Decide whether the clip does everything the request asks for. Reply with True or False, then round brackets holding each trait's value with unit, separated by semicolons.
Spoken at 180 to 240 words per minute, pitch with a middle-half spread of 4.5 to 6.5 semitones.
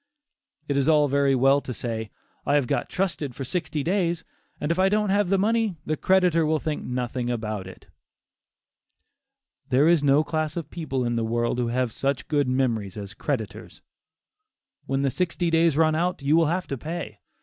True (190 wpm; 5.1 semitones)